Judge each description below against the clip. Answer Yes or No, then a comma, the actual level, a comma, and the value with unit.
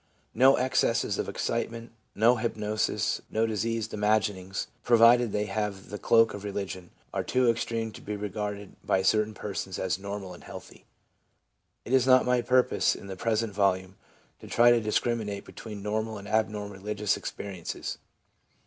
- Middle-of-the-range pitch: No, low, 105 Hz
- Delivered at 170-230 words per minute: No, average, 160 wpm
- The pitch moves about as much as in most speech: No, narrow, 2.3 semitones